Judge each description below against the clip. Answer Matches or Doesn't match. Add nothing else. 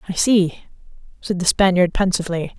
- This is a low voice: Doesn't match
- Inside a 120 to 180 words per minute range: Matches